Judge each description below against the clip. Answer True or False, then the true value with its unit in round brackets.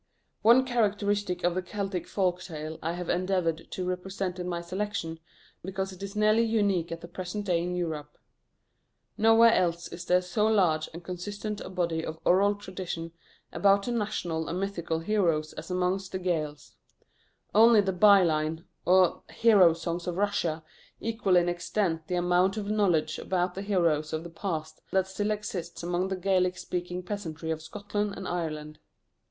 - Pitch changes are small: False (3.0 semitones)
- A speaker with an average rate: True (170 wpm)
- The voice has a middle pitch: True (180 Hz)